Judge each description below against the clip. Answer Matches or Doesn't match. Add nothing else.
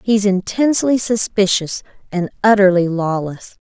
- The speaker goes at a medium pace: Doesn't match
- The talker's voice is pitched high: Matches